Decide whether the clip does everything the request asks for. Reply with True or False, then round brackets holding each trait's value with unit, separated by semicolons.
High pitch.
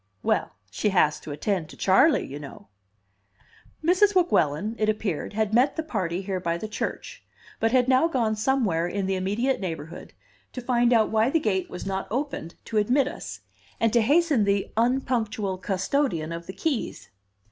True (215 Hz)